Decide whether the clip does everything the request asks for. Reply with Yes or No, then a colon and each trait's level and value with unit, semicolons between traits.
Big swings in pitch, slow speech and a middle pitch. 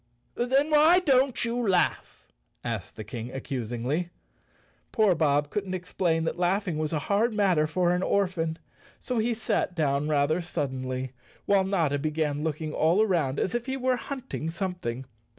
No: wide, 6.1 semitones; average, 160 wpm; medium, 175 Hz